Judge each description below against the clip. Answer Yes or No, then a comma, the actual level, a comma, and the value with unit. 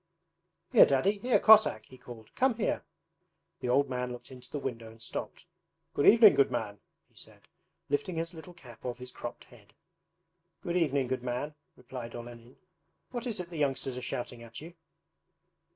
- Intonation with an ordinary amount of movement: No, wide, 5.8 semitones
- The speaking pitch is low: Yes, low, 130 Hz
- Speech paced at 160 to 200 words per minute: Yes, average, 175 wpm